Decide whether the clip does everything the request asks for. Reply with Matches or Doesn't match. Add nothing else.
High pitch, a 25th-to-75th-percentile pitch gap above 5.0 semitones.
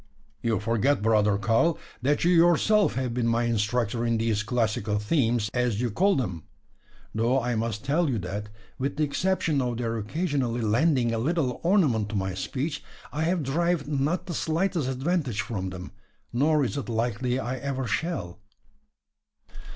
Doesn't match